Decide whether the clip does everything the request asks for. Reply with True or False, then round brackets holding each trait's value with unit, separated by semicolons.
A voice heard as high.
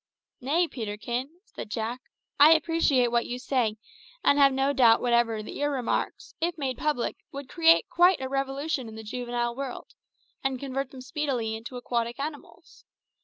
True (260 Hz)